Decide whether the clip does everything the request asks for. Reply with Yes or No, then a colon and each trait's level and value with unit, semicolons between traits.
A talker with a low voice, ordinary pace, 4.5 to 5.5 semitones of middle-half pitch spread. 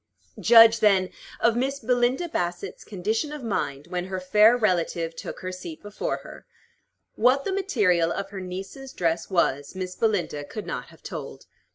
No: high, 195 Hz; average, 165 wpm; average, 4.9 semitones